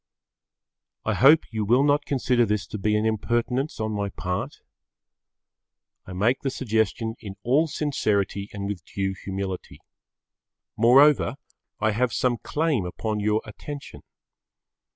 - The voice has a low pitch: Yes, low, 110 Hz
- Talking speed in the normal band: No, slow, 130 wpm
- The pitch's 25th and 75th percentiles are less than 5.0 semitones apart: Yes, average, 4.3 semitones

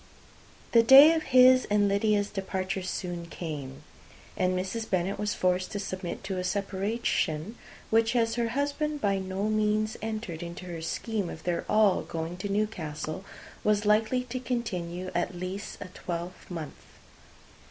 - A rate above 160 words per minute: No, average, 150 wpm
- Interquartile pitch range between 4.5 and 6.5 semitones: No, average, 3.7 semitones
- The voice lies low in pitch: No, high, 195 Hz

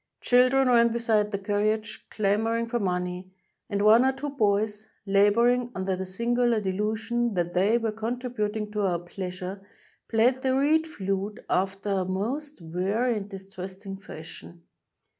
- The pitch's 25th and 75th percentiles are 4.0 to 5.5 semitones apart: No, average, 3.5 semitones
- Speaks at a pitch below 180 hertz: No, high, 210 Hz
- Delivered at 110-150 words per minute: Yes, average, 145 wpm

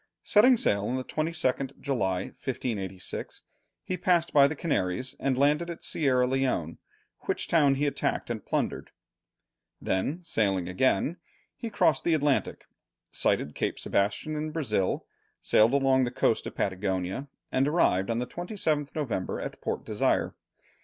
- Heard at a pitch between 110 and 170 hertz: Yes, low, 135 Hz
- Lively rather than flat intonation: Yes, wide, 7.4 semitones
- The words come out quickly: No, average, 145 wpm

